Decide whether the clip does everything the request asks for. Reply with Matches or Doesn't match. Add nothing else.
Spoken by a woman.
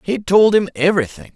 Doesn't match